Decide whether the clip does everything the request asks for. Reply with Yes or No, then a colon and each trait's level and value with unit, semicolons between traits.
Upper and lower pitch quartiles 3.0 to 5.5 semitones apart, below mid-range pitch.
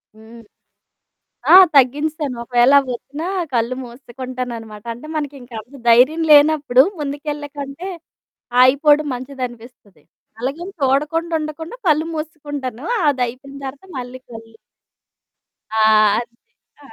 No: average, 3.4 semitones; very high, 270 Hz